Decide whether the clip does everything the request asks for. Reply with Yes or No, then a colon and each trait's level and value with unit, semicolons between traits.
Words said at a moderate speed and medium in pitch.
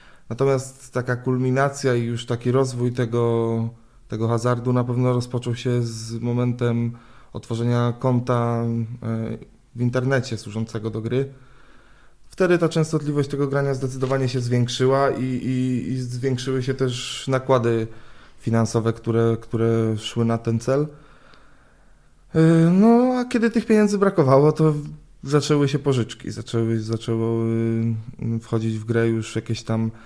No: average, 125 wpm; low, 125 Hz